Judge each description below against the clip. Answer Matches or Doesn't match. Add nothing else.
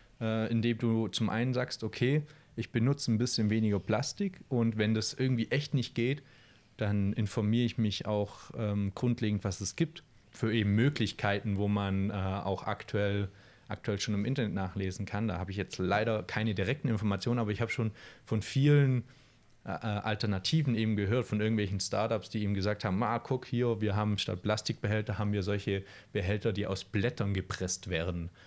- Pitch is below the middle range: Matches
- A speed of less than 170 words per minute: Doesn't match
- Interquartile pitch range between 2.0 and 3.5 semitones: Matches